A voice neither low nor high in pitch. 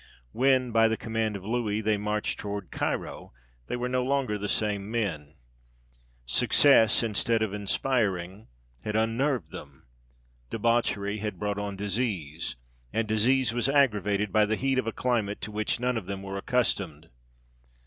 No: low, 110 Hz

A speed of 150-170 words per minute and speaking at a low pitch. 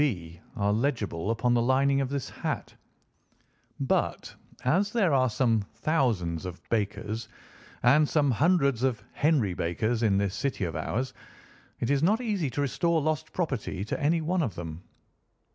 Yes: average, 160 wpm; low, 125 Hz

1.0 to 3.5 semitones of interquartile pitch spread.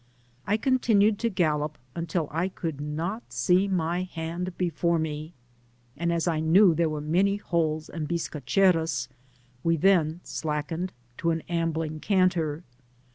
Yes: average, 2.7 semitones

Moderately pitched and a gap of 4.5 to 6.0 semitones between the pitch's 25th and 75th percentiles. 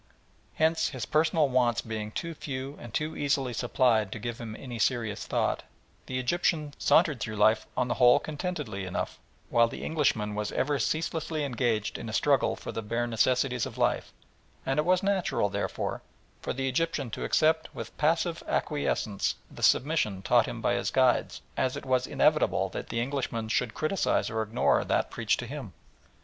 No: low, 125 Hz; average, 4.8 semitones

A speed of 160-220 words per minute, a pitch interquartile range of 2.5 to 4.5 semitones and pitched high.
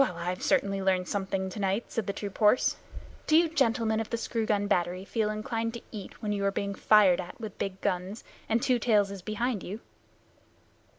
Yes: average, 200 wpm; average, 2.8 semitones; high, 205 Hz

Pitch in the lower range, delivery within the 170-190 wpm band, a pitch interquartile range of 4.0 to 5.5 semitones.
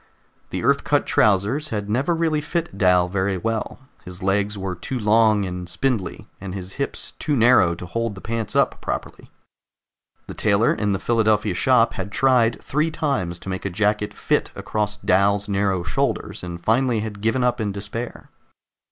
No: low, 105 Hz; average, 175 wpm; average, 3.6 semitones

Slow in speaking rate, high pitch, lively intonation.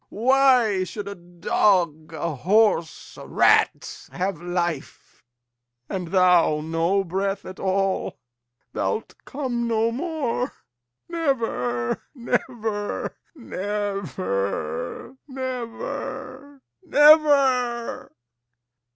Yes: slow, 80 wpm; high, 205 Hz; wide, 6.6 semitones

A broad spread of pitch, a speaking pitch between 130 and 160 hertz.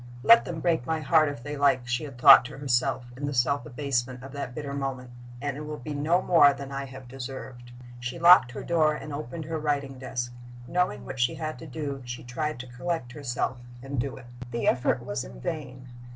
No: average, 3.4 semitones; low, 135 Hz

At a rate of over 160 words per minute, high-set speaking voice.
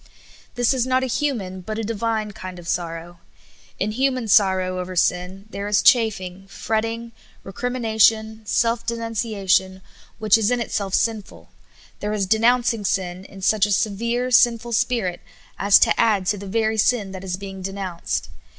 Yes: average, 180 wpm; high, 210 Hz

